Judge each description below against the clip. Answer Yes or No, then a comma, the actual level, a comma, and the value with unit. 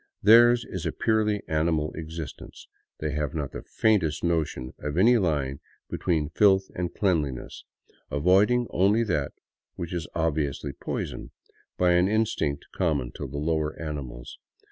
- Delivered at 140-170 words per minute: Yes, average, 145 wpm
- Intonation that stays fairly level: No, average, 4.6 semitones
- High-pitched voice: No, very low, 80 Hz